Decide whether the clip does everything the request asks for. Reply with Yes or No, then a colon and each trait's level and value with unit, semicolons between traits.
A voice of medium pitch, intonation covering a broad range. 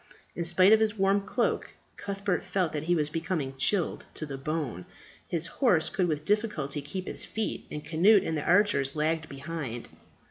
No: medium, 165 Hz; average, 4.8 semitones